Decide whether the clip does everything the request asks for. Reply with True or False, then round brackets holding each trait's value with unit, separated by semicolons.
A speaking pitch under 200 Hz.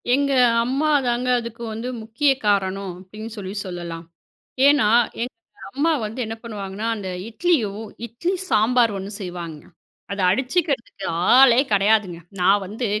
False (220 Hz)